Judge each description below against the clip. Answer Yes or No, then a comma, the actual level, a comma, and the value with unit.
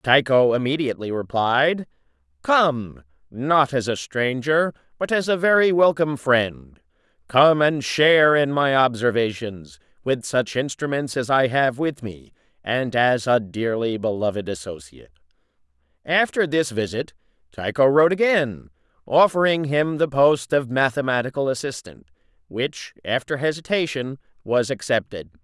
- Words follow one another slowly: Yes, slow, 125 wpm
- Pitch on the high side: No, low, 130 Hz